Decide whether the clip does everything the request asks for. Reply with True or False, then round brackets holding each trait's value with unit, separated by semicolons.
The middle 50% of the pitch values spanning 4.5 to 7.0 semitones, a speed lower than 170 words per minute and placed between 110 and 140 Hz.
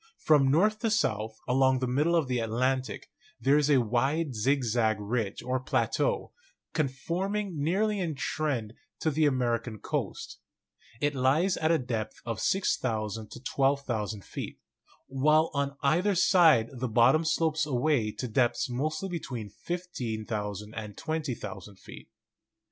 True (5.4 semitones; 140 wpm; 135 Hz)